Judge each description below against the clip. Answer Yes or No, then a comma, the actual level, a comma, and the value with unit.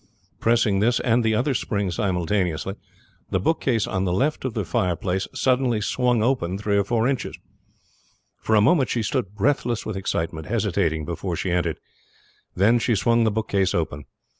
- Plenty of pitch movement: No, average, 4.3 semitones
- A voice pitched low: Yes, low, 105 Hz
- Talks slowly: No, average, 165 wpm